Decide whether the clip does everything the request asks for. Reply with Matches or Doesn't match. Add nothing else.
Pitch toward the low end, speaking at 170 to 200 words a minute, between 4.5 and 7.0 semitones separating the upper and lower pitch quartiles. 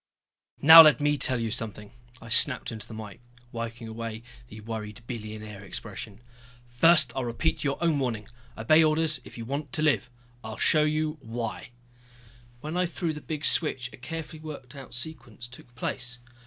Matches